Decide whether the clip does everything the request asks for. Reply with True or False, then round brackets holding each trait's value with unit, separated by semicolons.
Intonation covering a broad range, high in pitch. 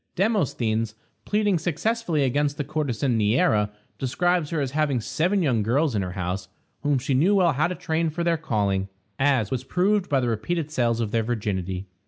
False (6.8 semitones; 140 Hz)